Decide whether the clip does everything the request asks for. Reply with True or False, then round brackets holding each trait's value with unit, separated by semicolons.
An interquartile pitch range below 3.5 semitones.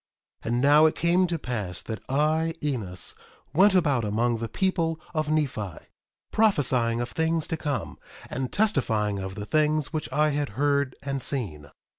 False (5.4 semitones)